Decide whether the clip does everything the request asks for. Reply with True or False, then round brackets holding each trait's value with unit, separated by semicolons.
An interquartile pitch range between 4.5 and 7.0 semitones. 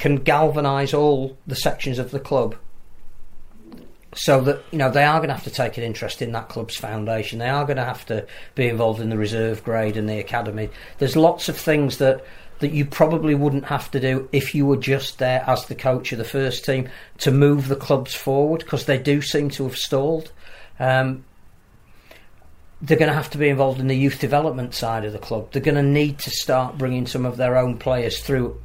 False (3.3 semitones)